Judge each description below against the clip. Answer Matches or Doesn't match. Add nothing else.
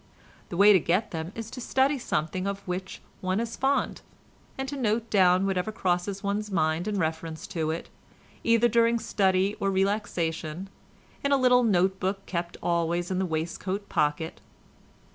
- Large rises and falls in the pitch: Doesn't match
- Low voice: Doesn't match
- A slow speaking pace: Doesn't match